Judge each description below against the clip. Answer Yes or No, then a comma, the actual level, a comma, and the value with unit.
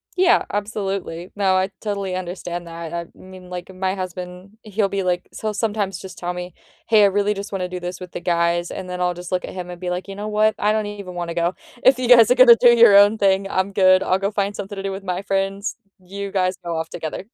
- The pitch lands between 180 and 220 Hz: Yes, high, 190 Hz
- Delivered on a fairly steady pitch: Yes, narrow, 2.2 semitones